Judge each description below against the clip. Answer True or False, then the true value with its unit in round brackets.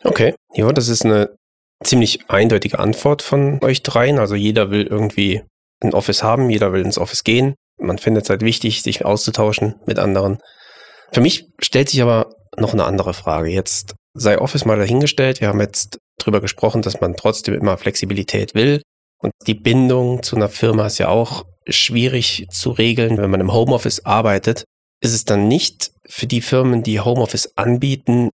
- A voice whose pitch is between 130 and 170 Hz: False (110 Hz)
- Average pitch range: True (3.2 semitones)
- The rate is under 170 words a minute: False (180 wpm)